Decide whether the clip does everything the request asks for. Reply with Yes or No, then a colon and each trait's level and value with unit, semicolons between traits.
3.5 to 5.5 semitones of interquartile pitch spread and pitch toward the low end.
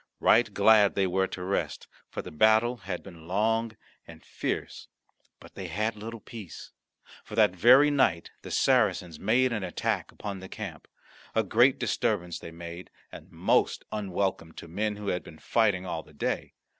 Yes: average, 3.8 semitones; low, 100 Hz